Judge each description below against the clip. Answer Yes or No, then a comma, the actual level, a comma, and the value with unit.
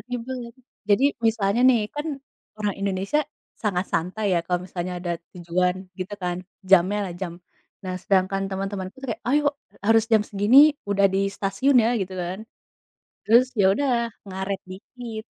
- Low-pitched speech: No, high, 200 Hz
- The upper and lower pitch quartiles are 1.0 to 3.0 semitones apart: No, average, 3.7 semitones